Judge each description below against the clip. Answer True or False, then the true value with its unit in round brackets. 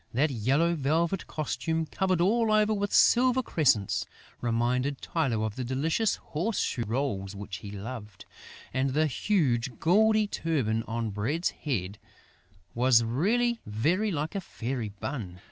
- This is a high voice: False (140 Hz)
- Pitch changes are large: True (7.4 semitones)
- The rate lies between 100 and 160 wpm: True (140 wpm)